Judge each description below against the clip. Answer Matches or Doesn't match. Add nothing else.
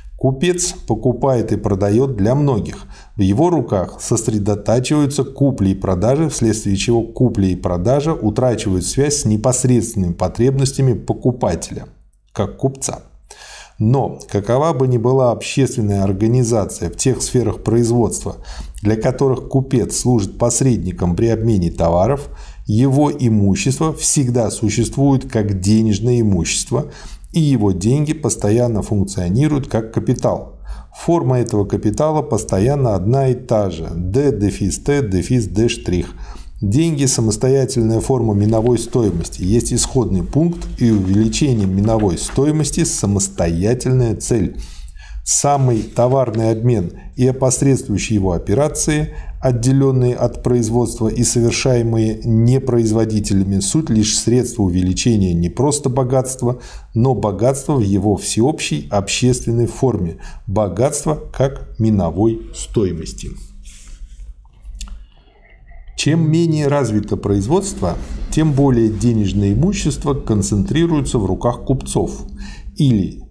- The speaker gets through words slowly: Matches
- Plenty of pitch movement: Doesn't match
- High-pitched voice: Doesn't match